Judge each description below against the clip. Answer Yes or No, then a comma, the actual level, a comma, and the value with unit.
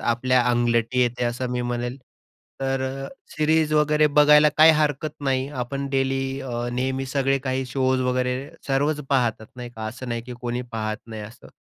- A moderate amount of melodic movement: No, narrow, 2.3 semitones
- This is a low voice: Yes, low, 130 Hz